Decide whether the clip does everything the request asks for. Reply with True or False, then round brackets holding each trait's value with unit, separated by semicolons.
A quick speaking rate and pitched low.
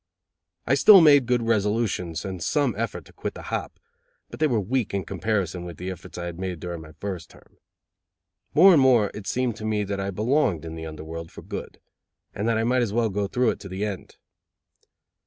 True (220 wpm; 105 Hz)